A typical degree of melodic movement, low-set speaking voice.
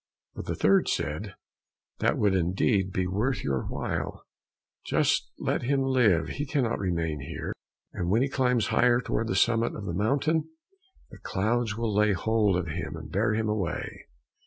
Yes: average, 4.9 semitones; low, 105 Hz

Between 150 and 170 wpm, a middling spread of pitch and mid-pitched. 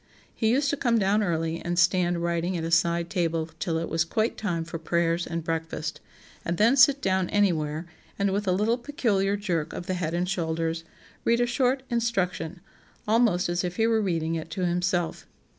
No: average, 195 wpm; average, 4.1 semitones; medium, 175 Hz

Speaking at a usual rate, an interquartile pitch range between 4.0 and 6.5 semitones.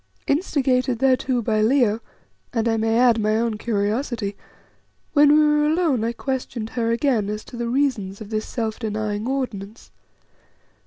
No: average, 155 wpm; average, 3.6 semitones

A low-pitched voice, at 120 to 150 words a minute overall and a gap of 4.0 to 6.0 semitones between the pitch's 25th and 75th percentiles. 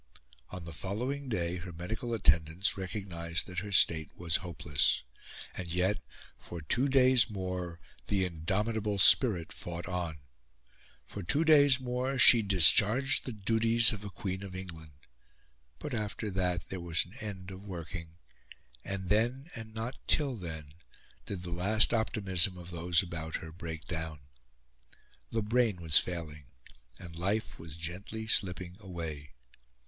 Yes: very low, 95 Hz; average, 145 wpm; average, 4.4 semitones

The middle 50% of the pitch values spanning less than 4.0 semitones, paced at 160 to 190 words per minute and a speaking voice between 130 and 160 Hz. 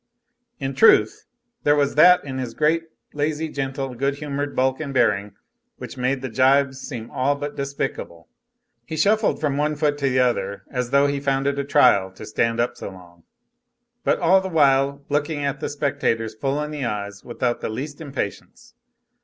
Yes: average, 2.9 semitones; average, 180 wpm; medium, 140 Hz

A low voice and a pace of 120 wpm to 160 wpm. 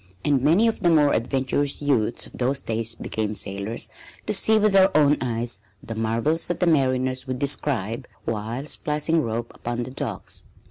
No: low, 130 Hz; average, 175 wpm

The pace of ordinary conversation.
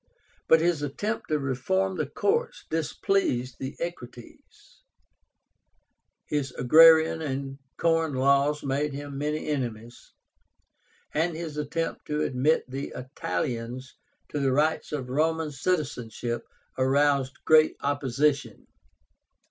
No: slow, 110 wpm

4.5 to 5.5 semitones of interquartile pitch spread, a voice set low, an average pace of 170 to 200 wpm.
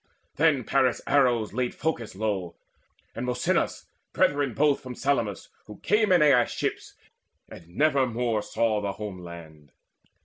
No: average, 5.2 semitones; low, 120 Hz; average, 140 wpm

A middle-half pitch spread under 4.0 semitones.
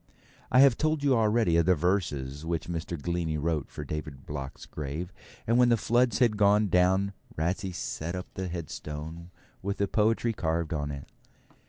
No: average, 5.1 semitones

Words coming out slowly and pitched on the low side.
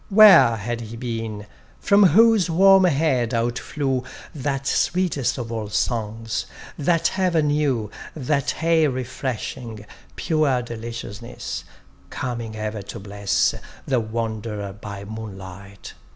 Yes: slow, 115 wpm; low, 120 Hz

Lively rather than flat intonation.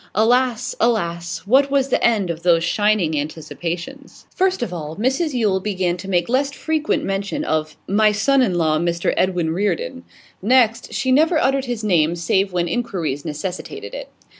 Yes: wide, 7.1 semitones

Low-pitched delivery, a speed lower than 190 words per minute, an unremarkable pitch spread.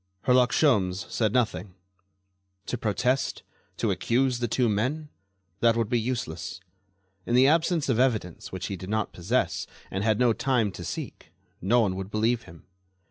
Yes: low, 115 Hz; average, 165 wpm; average, 4.3 semitones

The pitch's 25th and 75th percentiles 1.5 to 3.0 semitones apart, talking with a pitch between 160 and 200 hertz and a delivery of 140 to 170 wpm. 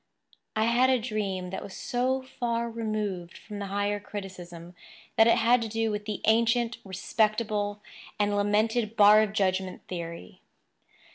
No: narrow, 2.6 semitones; high, 210 Hz; average, 150 wpm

